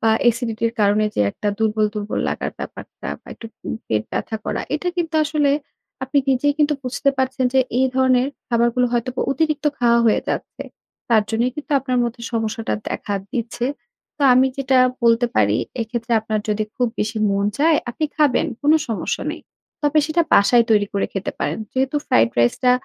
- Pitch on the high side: Yes, high, 240 Hz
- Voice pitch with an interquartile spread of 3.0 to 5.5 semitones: Yes, average, 3.5 semitones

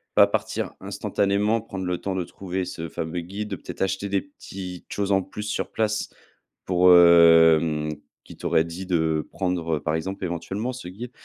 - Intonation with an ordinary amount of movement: Yes, average, 3.0 semitones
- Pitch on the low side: Yes, very low, 90 Hz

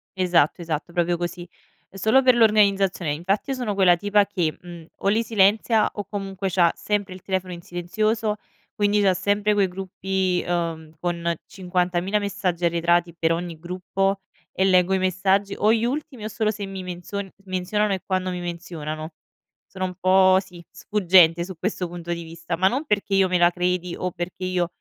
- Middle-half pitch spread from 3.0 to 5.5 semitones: No, narrow, 2.6 semitones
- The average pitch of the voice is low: No, medium, 185 Hz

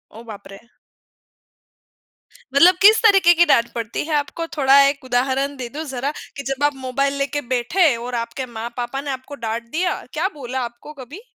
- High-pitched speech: Yes, very high, 270 Hz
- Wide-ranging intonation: No, average, 3.5 semitones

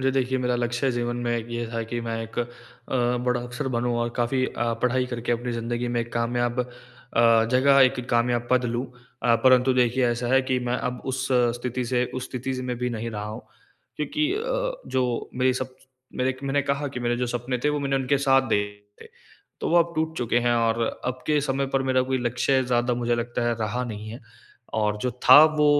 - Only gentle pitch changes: Yes, narrow, 1.7 semitones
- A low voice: Yes, low, 125 Hz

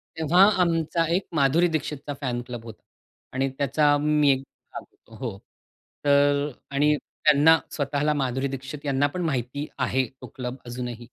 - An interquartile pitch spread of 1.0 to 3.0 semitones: Yes, narrow, 2.5 semitones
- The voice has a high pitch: No, medium, 140 Hz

